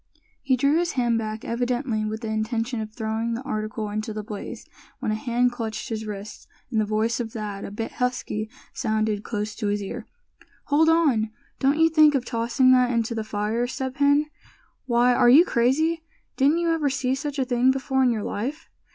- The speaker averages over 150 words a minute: Yes, average, 200 wpm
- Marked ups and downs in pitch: No, average, 3.6 semitones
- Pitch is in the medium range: No, high, 240 Hz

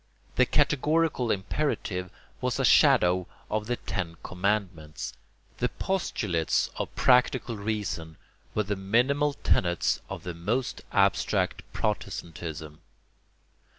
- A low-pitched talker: Yes, low, 105 Hz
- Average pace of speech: No, slow, 105 wpm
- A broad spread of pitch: Yes, wide, 6.3 semitones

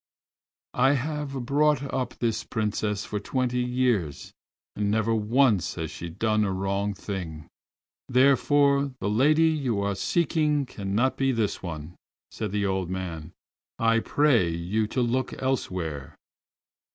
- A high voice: No, low, 115 Hz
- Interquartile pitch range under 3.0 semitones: No, average, 5.3 semitones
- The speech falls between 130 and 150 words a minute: Yes, slow, 135 wpm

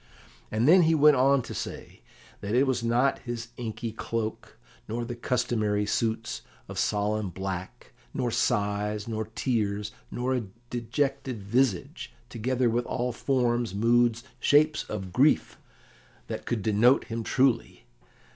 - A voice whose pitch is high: No, low, 115 Hz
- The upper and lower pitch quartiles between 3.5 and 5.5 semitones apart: No, average, 3.1 semitones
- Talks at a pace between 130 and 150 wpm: Yes, slow, 135 wpm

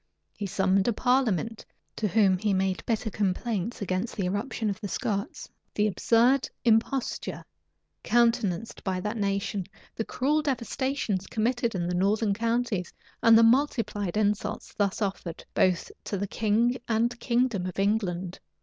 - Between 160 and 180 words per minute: No, average, 145 wpm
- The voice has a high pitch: Yes, high, 215 Hz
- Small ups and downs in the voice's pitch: No, average, 3.3 semitones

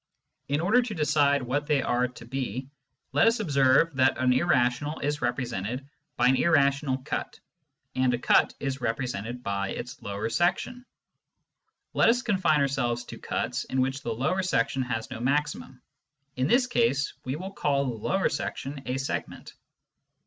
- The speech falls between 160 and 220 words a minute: Yes, average, 165 wpm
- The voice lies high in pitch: No, low, 135 Hz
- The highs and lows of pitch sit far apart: No, average, 3.5 semitones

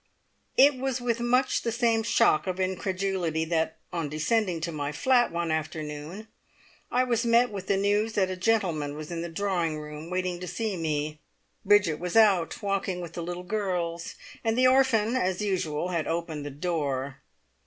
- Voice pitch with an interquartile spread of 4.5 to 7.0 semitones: Yes, average, 5.2 semitones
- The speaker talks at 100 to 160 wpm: No, average, 175 wpm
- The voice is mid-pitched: Yes, medium, 180 Hz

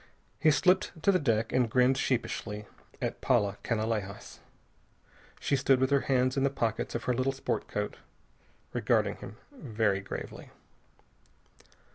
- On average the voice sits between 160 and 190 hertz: No, low, 125 Hz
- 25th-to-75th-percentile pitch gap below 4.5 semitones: Yes, average, 3.6 semitones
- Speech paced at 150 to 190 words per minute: No, average, 140 wpm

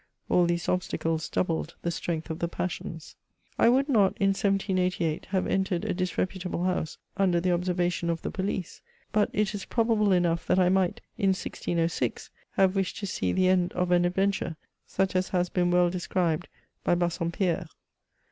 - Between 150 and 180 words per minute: Yes, average, 175 wpm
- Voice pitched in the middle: Yes, medium, 180 Hz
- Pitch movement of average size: No, narrow, 1.9 semitones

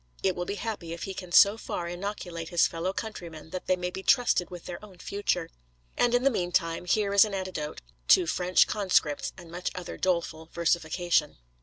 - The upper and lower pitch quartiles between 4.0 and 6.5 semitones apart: No, average, 2.7 semitones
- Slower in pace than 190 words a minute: No, average, 195 wpm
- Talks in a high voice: No, medium, 180 Hz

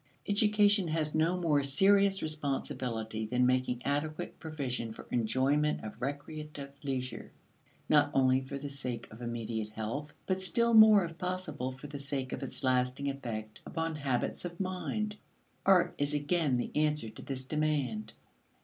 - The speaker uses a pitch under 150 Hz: Yes, medium, 140 Hz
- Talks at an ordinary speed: Yes, average, 150 wpm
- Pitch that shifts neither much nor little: Yes, average, 4.3 semitones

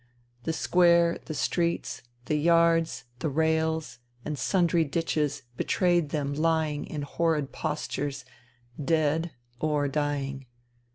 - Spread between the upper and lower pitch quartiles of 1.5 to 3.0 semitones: Yes, narrow, 2.4 semitones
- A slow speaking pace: Yes, slow, 110 wpm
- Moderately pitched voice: Yes, medium, 155 Hz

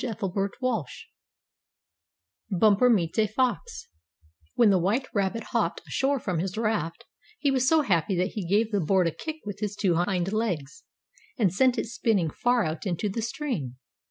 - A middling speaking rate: Yes, average, 170 wpm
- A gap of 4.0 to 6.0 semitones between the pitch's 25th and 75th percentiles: Yes, average, 4.7 semitones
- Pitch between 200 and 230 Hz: Yes, high, 205 Hz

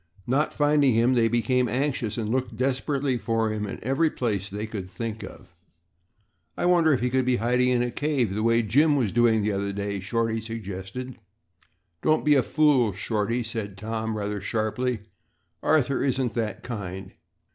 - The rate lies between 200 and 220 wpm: No, average, 175 wpm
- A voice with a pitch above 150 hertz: No, low, 115 Hz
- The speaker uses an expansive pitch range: No, average, 3.3 semitones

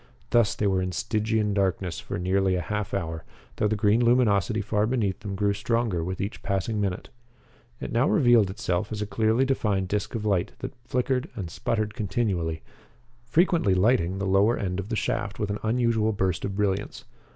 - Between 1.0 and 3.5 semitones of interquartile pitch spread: Yes, average, 3.0 semitones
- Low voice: Yes, low, 105 Hz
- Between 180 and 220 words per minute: Yes, average, 185 wpm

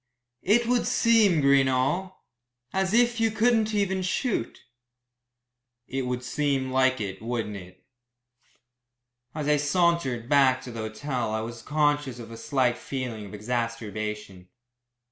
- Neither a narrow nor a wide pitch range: No, wide, 7.4 semitones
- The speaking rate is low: Yes, slow, 130 wpm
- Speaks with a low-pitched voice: Yes, low, 130 Hz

